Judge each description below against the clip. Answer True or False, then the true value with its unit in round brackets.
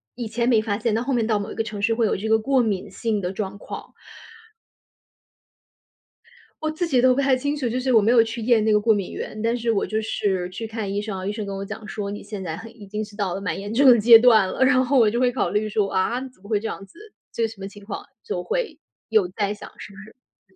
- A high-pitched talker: True (220 Hz)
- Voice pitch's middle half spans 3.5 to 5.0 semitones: False (2.8 semitones)